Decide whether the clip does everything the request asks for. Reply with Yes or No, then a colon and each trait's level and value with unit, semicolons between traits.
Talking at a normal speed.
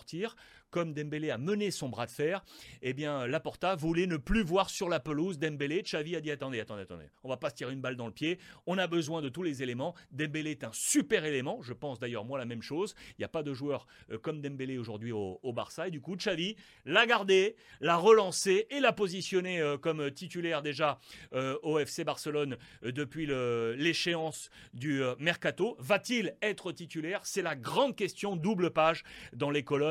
Yes: average, 195 wpm